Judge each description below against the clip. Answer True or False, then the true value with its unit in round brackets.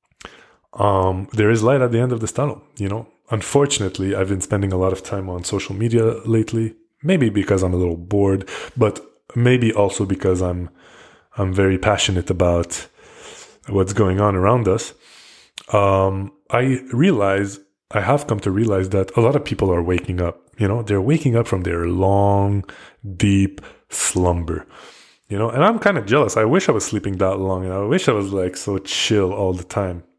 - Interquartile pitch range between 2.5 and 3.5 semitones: True (3.2 semitones)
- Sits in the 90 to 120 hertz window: True (100 Hz)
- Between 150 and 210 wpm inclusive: True (190 wpm)